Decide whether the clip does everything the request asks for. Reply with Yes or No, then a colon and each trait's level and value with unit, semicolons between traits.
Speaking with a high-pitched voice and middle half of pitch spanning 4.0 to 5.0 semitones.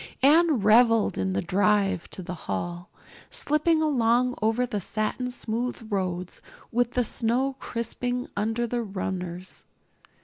Yes: high, 225 Hz; average, 4.5 semitones